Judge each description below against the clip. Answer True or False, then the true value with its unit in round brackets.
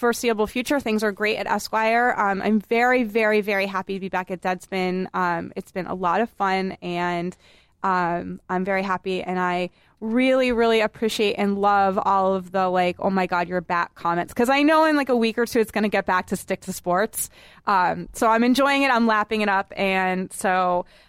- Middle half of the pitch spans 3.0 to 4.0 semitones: True (3.5 semitones)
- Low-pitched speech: False (195 Hz)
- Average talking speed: False (215 wpm)